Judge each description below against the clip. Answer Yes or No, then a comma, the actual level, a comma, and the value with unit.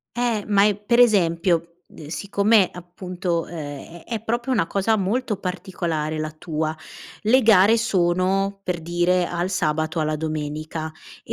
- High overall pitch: No, medium, 180 Hz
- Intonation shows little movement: No, average, 4.1 semitones